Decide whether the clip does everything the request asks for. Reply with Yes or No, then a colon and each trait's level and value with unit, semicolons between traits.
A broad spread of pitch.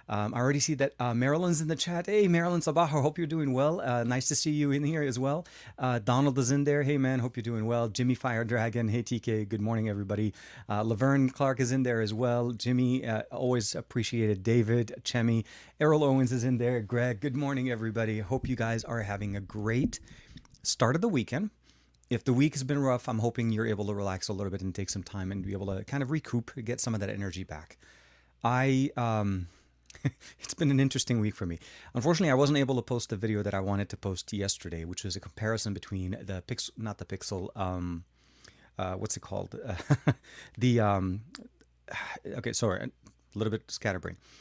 No: average, 4.5 semitones